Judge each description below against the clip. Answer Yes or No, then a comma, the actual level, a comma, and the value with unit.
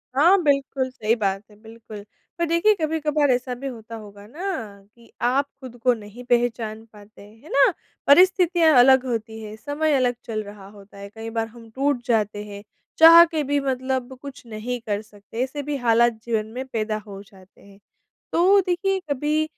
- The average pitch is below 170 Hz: No, high, 245 Hz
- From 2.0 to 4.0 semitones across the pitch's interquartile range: No, average, 5.0 semitones